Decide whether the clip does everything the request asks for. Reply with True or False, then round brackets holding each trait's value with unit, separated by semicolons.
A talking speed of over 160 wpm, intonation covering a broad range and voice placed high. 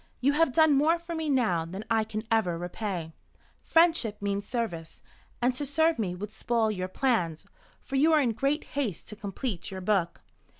True (185 wpm; 6.9 semitones; 225 Hz)